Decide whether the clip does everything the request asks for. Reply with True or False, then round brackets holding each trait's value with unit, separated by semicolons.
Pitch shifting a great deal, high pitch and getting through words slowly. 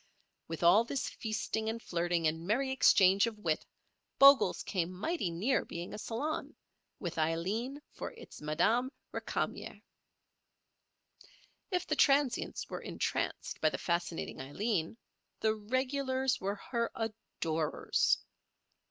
True (7.1 semitones; 215 Hz; 120 wpm)